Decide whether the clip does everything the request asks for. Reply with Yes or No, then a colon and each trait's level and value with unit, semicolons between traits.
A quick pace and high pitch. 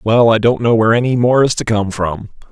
No: fast, 260 wpm; low, 115 Hz